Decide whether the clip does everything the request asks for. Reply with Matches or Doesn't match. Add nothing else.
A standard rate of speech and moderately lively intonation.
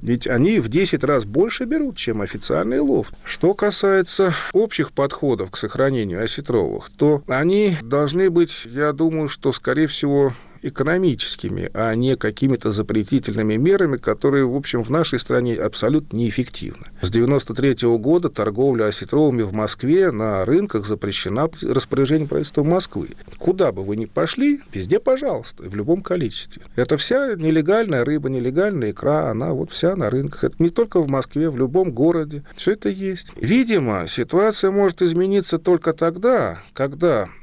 Doesn't match